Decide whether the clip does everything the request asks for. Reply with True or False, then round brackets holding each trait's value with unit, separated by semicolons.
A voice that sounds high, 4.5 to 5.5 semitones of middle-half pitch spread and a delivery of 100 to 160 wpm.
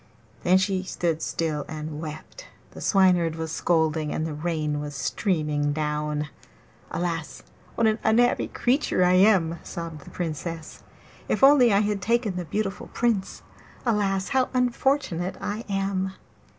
False (180 Hz; 4.8 semitones; 140 wpm)